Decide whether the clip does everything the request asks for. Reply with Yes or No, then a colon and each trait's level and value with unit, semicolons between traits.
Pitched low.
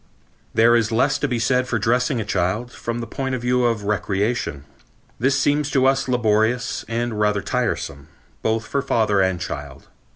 Yes: low, 115 Hz